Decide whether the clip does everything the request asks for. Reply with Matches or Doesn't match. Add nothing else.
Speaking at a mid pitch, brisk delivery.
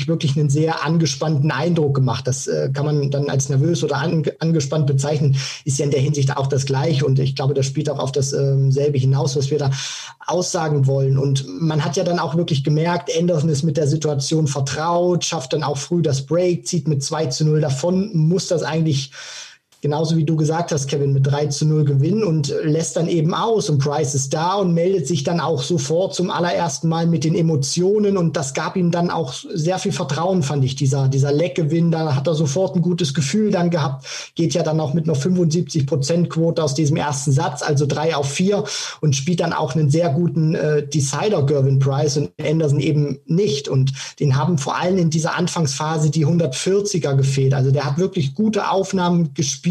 Matches